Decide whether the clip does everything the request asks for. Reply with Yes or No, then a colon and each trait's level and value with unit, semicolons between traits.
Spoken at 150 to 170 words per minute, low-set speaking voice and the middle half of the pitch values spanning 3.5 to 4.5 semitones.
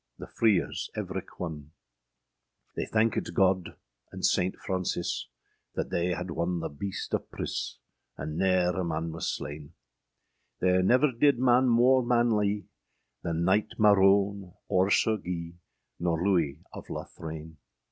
No: slow, 135 wpm; very low, 95 Hz; average, 3.8 semitones